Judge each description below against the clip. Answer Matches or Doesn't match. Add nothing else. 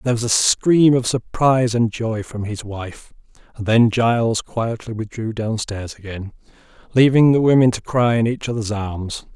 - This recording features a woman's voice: Doesn't match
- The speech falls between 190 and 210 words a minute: Doesn't match